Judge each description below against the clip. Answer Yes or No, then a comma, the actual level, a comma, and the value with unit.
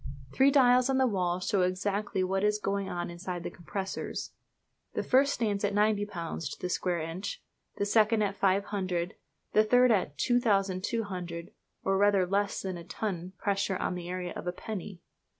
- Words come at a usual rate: Yes, average, 180 wpm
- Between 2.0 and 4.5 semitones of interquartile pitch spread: Yes, average, 2.7 semitones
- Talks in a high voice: Yes, high, 195 Hz